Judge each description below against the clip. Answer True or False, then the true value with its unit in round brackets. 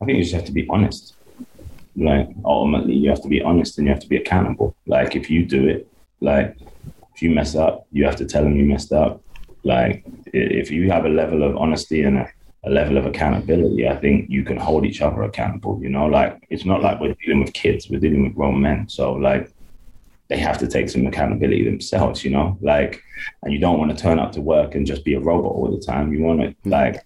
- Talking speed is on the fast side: True (240 wpm)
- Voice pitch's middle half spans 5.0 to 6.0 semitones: False (2.5 semitones)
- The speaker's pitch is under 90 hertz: True (70 Hz)